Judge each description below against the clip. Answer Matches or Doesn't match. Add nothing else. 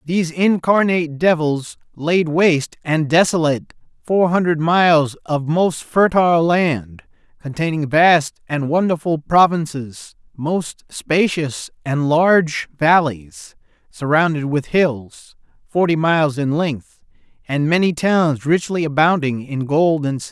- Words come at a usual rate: Doesn't match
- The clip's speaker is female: Doesn't match